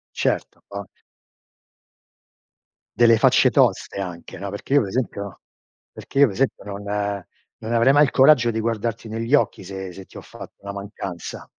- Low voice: Yes, low, 105 Hz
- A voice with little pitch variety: No, average, 3.0 semitones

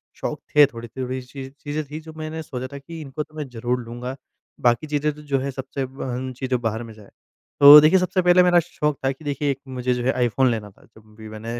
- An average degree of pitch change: Yes, average, 3.5 semitones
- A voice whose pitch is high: No, low, 135 Hz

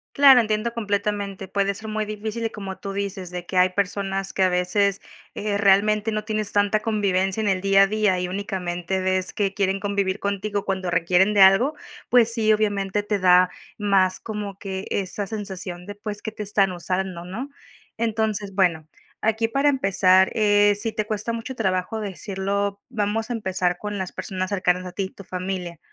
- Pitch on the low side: No, high, 200 Hz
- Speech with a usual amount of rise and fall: No, narrow, 2.1 semitones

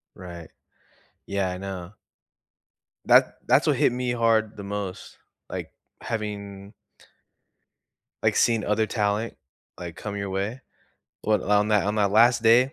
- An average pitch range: No, narrow, 2.2 semitones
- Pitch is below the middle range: Yes, low, 105 Hz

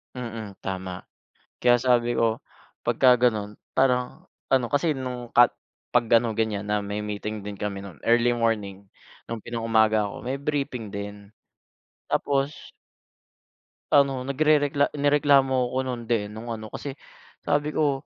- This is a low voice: Yes, low, 120 Hz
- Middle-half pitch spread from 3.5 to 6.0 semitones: Yes, average, 4.1 semitones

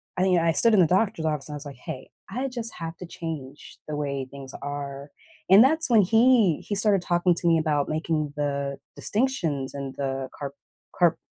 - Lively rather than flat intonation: Yes, wide, 5.8 semitones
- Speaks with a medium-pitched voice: Yes, medium, 160 Hz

